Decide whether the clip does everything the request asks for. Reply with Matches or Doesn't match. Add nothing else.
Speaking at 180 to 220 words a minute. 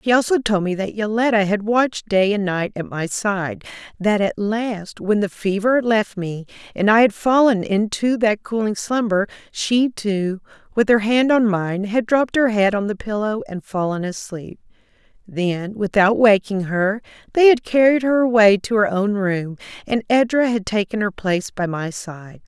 Matches